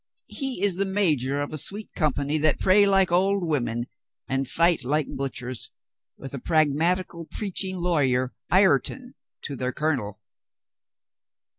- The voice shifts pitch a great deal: Yes, wide, 5.7 semitones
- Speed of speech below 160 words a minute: Yes, slow, 135 wpm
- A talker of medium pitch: Yes, medium, 155 Hz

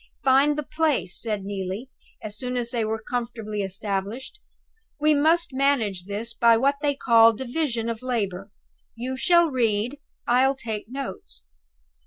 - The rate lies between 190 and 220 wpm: No, average, 155 wpm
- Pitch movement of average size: Yes, average, 4.4 semitones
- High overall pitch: Yes, high, 235 Hz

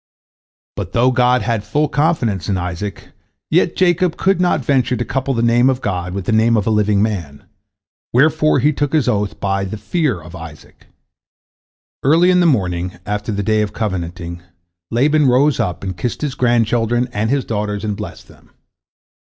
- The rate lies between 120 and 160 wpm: No, average, 180 wpm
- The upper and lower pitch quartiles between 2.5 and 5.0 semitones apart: No, wide, 5.5 semitones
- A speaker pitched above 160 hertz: No, low, 115 Hz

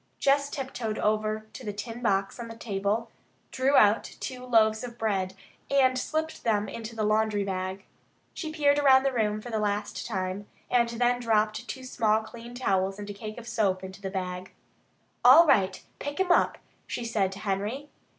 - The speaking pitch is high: Yes, high, 220 Hz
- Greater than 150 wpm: Yes, average, 190 wpm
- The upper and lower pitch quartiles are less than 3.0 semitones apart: No, average, 3.4 semitones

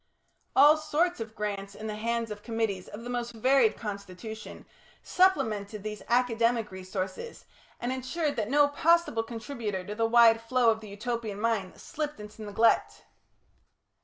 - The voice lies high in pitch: Yes, high, 225 Hz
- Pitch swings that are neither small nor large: Yes, average, 3.0 semitones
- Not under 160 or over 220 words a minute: No, average, 150 wpm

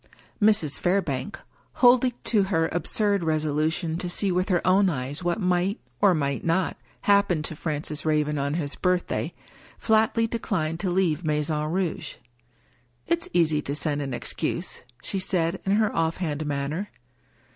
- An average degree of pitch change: Yes, average, 4.2 semitones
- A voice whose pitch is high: No, medium, 170 Hz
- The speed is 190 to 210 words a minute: No, average, 165 wpm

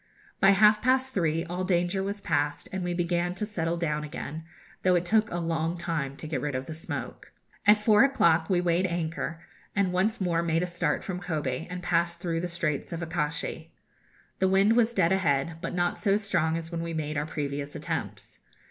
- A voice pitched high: No, medium, 170 Hz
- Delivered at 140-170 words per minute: No, fast, 205 wpm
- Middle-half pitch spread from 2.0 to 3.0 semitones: Yes, average, 2.7 semitones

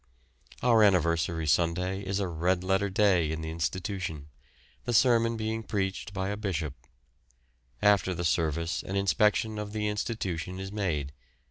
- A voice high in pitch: No, very low, 95 Hz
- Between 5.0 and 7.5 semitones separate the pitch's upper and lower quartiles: No, average, 3.8 semitones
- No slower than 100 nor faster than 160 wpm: Yes, average, 145 wpm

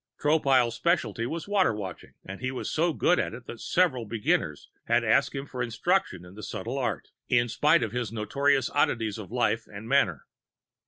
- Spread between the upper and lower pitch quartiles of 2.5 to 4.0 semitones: No, average, 4.5 semitones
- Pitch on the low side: Yes, low, 120 Hz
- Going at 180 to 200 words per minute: Yes, average, 190 wpm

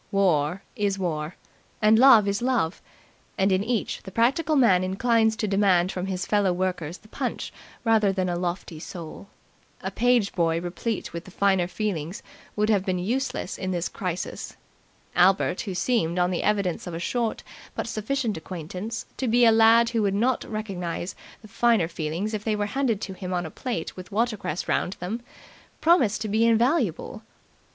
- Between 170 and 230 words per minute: Yes, average, 175 wpm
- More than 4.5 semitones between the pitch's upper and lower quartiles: No, average, 3.9 semitones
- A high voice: Yes, high, 200 Hz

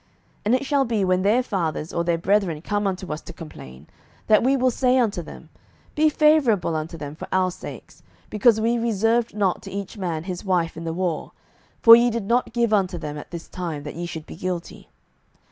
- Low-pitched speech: No, high, 190 Hz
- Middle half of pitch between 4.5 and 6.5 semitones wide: Yes, wide, 5.5 semitones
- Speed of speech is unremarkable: No, fast, 215 wpm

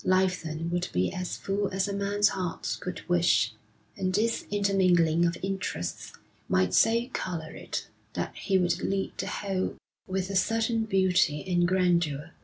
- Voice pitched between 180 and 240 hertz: Yes, medium, 185 Hz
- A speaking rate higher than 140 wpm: Yes, average, 160 wpm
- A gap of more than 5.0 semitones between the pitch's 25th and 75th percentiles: No, narrow, 2.5 semitones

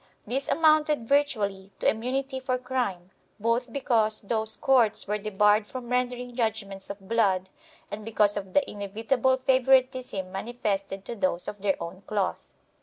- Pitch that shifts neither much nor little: Yes, average, 4.3 semitones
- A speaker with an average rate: Yes, average, 145 wpm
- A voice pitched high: Yes, high, 225 Hz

